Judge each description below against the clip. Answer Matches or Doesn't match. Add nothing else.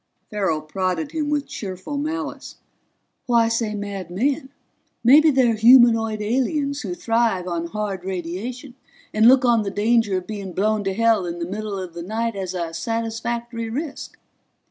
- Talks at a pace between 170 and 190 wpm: Doesn't match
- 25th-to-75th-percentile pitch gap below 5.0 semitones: Matches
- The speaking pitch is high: Matches